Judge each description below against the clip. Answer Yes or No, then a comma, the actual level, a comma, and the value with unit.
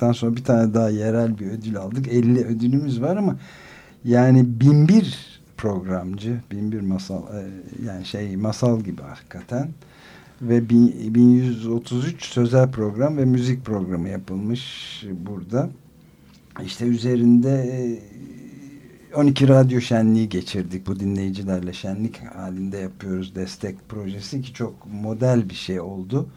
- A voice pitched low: Yes, low, 115 Hz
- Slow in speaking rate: No, average, 115 wpm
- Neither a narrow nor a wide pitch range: Yes, average, 4.4 semitones